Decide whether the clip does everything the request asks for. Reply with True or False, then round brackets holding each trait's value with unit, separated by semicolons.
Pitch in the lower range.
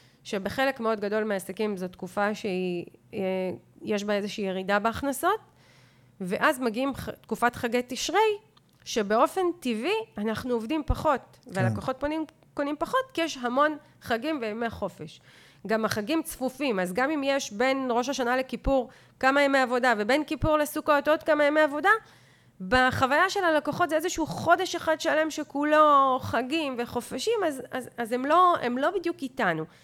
False (260 Hz)